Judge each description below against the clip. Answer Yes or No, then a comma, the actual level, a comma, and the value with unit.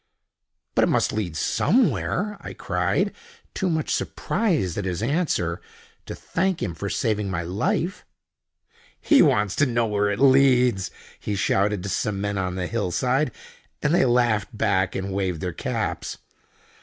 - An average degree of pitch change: No, wide, 5.7 semitones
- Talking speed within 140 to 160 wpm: Yes, average, 155 wpm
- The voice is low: Yes, low, 105 Hz